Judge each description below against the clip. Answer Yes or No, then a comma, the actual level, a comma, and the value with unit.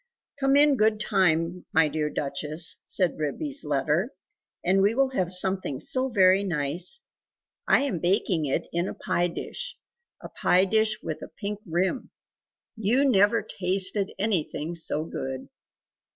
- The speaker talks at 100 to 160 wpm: Yes, average, 145 wpm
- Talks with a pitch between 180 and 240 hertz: Yes, medium, 185 Hz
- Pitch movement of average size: Yes, average, 5.0 semitones